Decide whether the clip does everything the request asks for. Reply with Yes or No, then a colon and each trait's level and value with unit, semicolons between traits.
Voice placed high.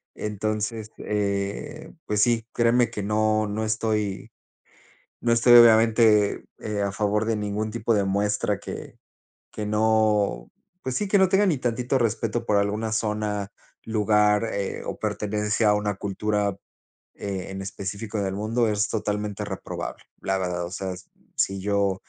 No: low, 105 Hz